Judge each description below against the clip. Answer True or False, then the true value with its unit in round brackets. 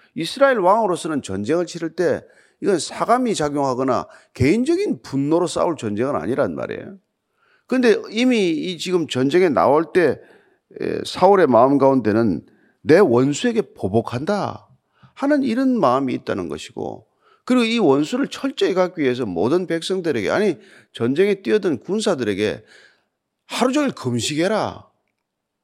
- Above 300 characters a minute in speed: True (310 characters per minute)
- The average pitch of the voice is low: False (185 Hz)